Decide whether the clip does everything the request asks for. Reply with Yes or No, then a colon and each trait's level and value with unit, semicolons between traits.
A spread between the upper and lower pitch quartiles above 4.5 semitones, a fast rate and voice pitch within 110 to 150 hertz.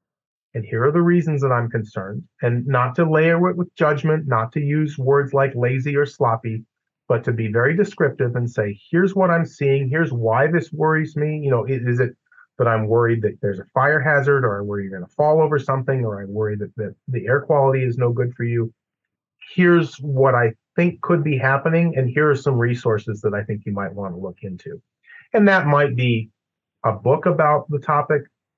Yes: average, 5.0 semitones; fast, 215 wpm; low, 135 Hz